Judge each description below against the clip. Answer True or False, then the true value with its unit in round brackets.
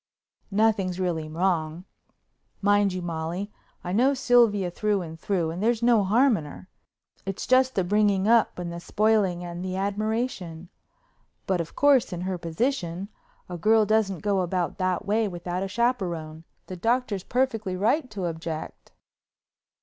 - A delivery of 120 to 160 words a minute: True (150 wpm)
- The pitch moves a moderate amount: True (3.9 semitones)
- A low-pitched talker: False (195 Hz)